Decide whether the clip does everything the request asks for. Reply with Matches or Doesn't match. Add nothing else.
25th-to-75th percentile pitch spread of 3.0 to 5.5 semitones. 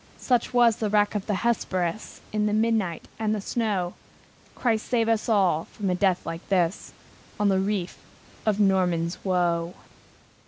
Matches